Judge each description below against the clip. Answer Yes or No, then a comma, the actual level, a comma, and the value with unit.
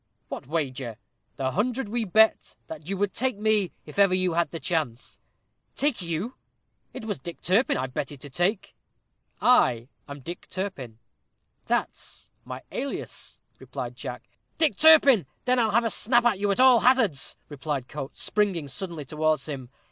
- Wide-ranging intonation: Yes, wide, 7.4 semitones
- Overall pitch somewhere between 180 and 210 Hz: Yes, medium, 185 Hz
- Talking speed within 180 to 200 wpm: No, average, 165 wpm